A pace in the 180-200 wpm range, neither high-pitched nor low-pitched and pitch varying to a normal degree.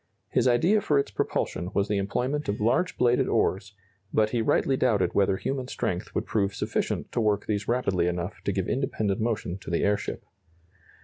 No: average, 185 wpm; low, 105 Hz; average, 4.3 semitones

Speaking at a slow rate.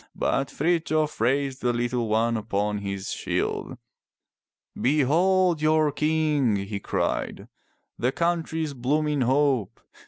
Yes: slow, 105 wpm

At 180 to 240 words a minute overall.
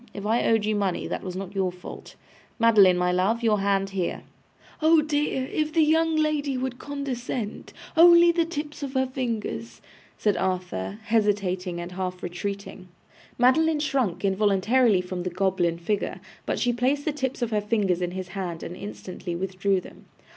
No: average, 170 wpm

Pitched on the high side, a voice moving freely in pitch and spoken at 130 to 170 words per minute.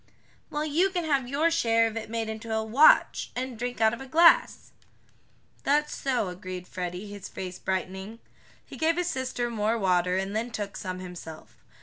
No: high, 225 Hz; wide, 6.1 semitones; average, 185 wpm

